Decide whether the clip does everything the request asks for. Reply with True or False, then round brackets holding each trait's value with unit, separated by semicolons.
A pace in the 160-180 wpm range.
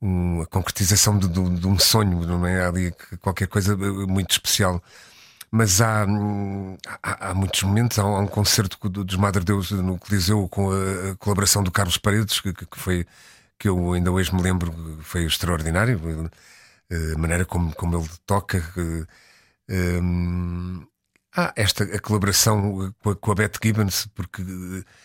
True (170 wpm)